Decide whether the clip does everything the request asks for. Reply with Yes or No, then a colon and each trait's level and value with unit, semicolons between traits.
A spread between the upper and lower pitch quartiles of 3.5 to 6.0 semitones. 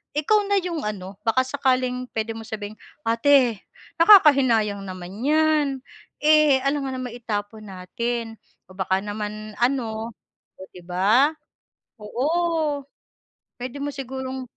Yes: average, 5.1 semitones